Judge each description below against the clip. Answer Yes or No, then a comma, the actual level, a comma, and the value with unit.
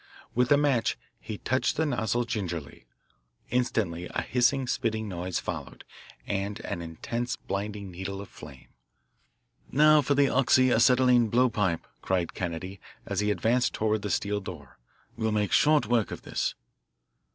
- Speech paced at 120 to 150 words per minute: Yes, average, 145 wpm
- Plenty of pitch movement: No, average, 4.7 semitones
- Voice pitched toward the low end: Yes, low, 110 Hz